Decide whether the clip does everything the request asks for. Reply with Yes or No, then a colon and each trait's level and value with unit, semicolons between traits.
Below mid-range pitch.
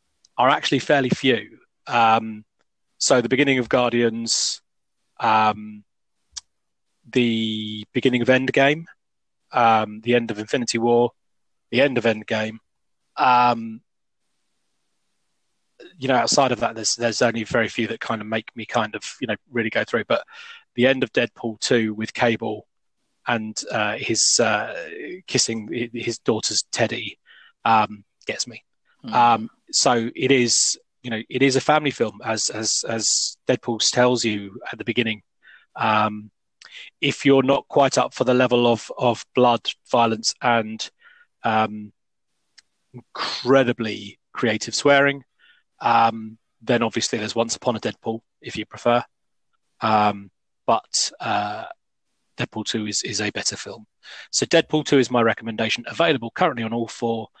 Yes: low, 115 Hz